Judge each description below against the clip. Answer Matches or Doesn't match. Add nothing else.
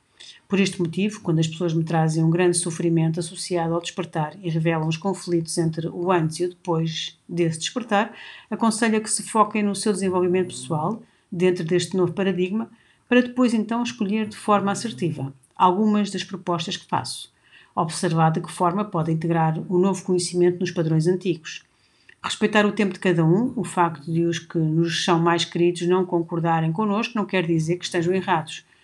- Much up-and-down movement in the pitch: Doesn't match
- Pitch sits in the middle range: Matches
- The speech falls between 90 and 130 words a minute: Doesn't match